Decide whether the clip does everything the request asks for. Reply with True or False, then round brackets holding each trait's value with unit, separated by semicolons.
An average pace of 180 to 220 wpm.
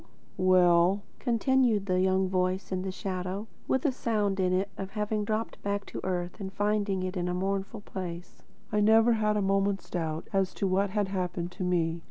True (190 wpm)